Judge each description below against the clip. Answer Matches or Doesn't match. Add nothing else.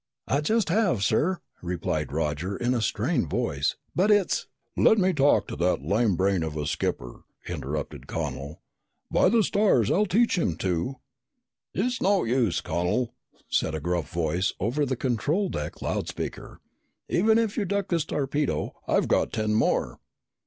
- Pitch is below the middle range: Matches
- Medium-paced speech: Matches